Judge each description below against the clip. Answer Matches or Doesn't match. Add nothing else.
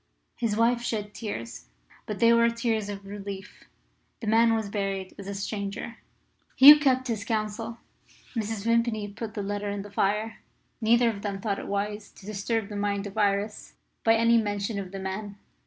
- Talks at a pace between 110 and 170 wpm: Doesn't match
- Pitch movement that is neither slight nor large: Doesn't match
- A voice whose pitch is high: Matches